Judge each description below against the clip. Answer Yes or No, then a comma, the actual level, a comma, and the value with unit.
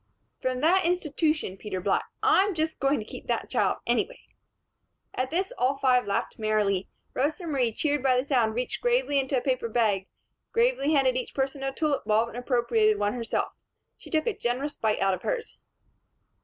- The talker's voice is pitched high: Yes, very high, 260 Hz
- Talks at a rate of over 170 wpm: Yes, average, 185 wpm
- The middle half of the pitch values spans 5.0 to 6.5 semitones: Yes, wide, 5.4 semitones